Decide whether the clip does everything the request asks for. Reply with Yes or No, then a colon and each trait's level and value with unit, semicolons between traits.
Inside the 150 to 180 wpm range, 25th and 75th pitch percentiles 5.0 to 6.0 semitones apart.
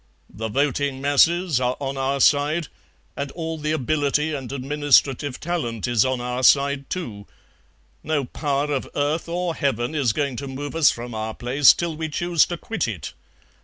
No: average, 170 wpm; average, 3.4 semitones